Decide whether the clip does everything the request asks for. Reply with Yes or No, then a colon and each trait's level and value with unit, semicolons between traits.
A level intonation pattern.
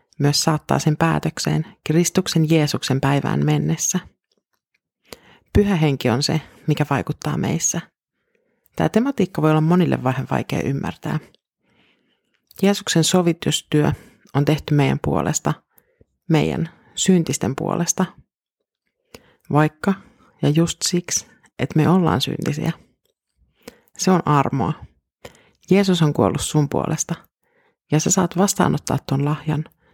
No: average, 4.1 semitones